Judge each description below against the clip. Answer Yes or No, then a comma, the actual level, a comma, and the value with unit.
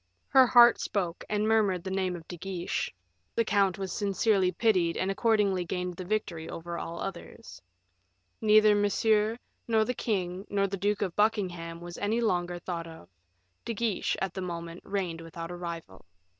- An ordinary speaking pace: Yes, average, 170 wpm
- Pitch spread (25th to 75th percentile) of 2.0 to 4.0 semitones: Yes, average, 3.4 semitones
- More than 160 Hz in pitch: Yes, high, 190 Hz